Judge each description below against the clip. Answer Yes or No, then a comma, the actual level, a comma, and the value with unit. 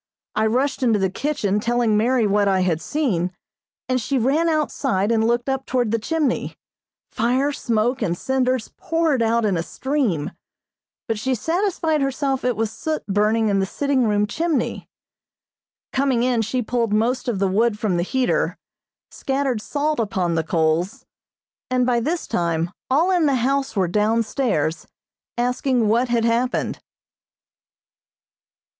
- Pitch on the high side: Yes, high, 235 Hz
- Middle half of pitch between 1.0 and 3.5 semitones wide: No, average, 4.3 semitones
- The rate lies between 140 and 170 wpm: Yes, average, 155 wpm